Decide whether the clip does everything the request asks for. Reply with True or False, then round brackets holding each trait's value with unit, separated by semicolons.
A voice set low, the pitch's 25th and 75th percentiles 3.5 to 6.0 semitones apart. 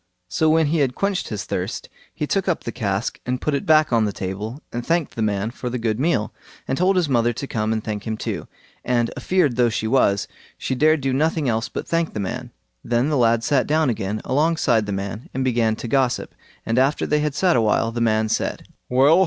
True (125 Hz; 5.3 semitones)